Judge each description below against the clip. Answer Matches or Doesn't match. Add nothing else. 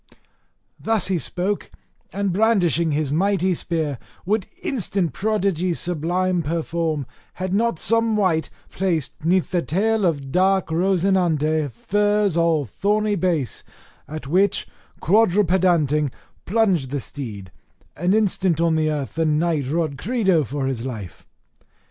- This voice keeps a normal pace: Doesn't match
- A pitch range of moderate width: Matches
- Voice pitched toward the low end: Doesn't match